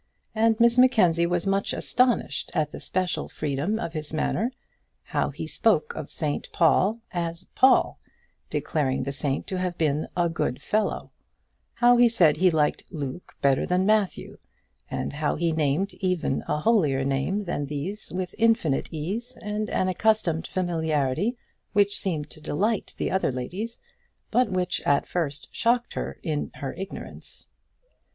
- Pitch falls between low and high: Yes, medium, 180 Hz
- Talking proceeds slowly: No, average, 155 wpm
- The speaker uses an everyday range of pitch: No, wide, 5.8 semitones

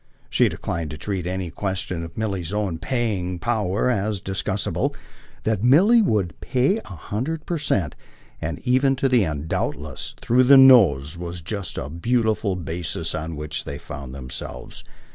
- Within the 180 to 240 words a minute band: No, average, 160 wpm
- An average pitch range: No, wide, 6.6 semitones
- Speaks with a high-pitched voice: No, very low, 95 Hz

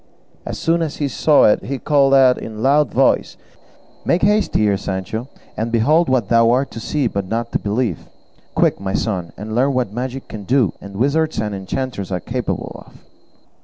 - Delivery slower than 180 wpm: No, average, 195 wpm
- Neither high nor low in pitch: No, low, 120 Hz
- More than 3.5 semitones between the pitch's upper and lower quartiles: Yes, average, 4.6 semitones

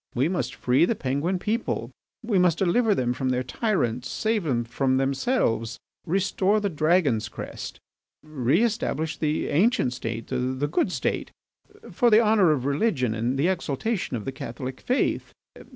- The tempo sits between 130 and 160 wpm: Yes, average, 150 wpm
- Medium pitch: Yes, medium, 150 Hz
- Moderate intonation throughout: No, wide, 7.4 semitones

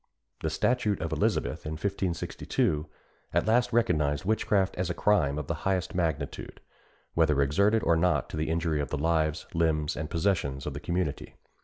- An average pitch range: Yes, average, 4.1 semitones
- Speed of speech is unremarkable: Yes, average, 170 wpm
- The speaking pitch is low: Yes, very low, 85 Hz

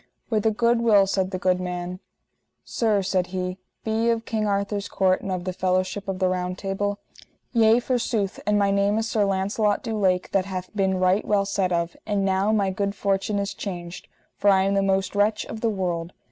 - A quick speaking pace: Yes, fast, 215 wpm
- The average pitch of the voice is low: No, high, 195 Hz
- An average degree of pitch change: No, narrow, 2.1 semitones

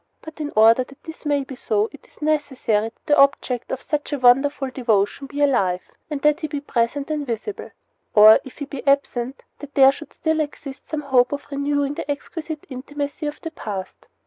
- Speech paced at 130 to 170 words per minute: No, average, 200 wpm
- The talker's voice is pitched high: Yes, very high, 280 Hz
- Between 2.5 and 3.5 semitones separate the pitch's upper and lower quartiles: Yes, average, 2.9 semitones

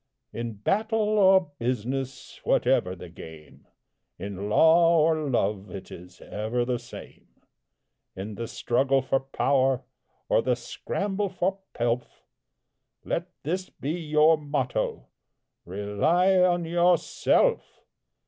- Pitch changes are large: Yes, wide, 7.9 semitones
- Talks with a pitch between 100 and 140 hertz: Yes, low, 135 Hz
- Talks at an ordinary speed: No, slow, 110 wpm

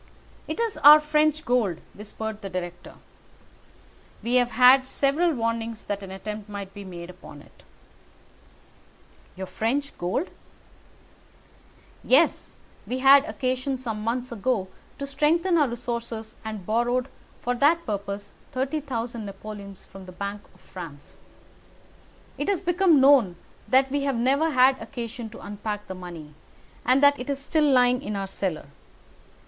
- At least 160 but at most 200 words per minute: No, average, 140 wpm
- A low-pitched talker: No, high, 240 Hz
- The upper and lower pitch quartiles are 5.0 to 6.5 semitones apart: Yes, average, 5.3 semitones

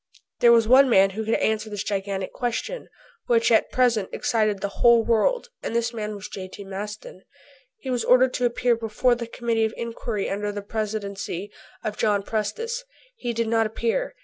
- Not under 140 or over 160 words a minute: No, average, 180 wpm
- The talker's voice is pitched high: Yes, high, 225 Hz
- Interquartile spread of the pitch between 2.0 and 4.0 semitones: Yes, narrow, 2.6 semitones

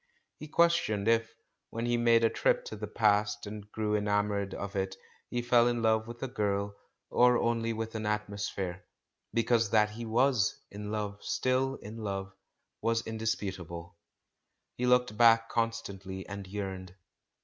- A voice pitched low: Yes, low, 110 Hz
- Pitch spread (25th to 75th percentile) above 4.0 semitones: No, narrow, 2.6 semitones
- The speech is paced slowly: No, average, 155 wpm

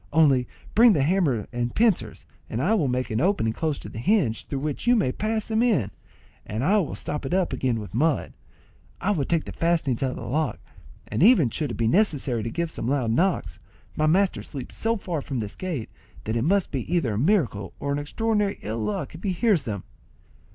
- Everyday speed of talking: No, fast, 225 wpm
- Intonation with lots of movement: Yes, wide, 7.9 semitones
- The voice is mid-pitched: Yes, medium, 150 Hz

